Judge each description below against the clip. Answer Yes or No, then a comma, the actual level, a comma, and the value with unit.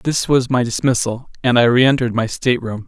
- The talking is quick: No, average, 190 wpm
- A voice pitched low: Yes, low, 125 Hz